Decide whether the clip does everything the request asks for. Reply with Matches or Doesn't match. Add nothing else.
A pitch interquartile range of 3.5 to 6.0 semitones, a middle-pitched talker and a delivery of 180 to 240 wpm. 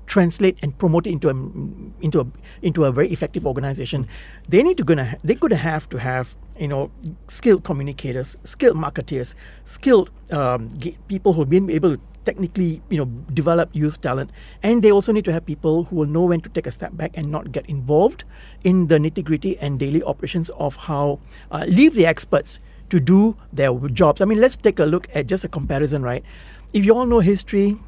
Matches